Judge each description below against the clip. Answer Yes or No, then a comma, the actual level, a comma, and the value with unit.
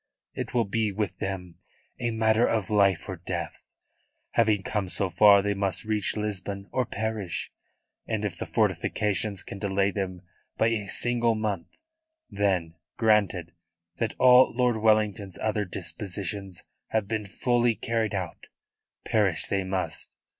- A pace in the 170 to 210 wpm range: No, average, 140 wpm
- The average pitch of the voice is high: No, low, 105 Hz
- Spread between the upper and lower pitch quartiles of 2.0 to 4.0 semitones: Yes, narrow, 2.5 semitones